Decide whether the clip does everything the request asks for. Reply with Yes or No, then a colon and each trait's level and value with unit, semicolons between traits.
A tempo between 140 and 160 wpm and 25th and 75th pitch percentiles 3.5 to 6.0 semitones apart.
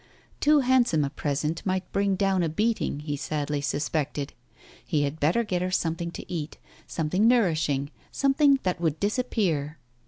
Yes: average, 155 wpm; wide, 5.5 semitones